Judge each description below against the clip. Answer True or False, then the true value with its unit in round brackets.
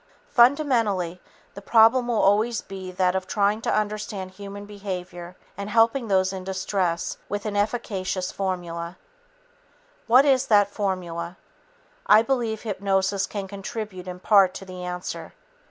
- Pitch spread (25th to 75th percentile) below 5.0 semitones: True (2.8 semitones)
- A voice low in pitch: False (200 Hz)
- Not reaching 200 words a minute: True (140 wpm)